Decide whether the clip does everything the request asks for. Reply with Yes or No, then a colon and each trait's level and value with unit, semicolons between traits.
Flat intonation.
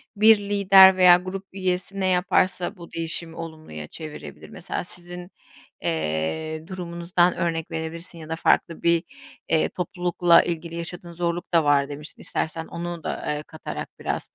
Yes: narrow, 2.1 semitones